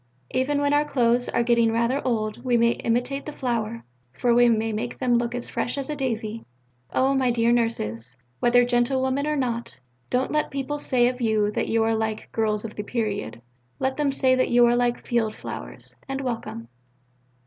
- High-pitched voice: Yes, high, 240 Hz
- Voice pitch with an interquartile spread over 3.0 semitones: No, narrow, 2.5 semitones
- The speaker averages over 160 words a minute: Yes, average, 195 wpm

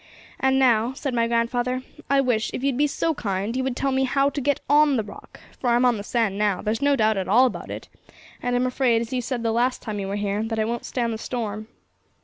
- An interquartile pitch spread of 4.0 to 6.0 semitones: No, average, 3.2 semitones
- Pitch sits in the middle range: No, high, 240 Hz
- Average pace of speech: No, fast, 260 wpm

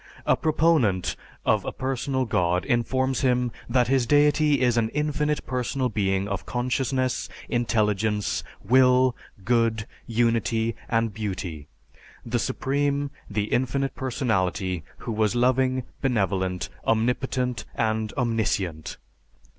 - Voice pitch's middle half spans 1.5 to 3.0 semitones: No, average, 3.6 semitones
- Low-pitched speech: Yes, low, 120 Hz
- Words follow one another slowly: Yes, slow, 110 wpm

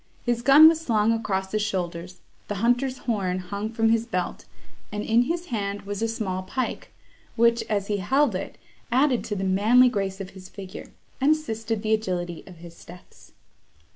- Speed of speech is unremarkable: Yes, average, 180 wpm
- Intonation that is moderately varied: Yes, average, 3.7 semitones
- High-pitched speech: Yes, high, 215 Hz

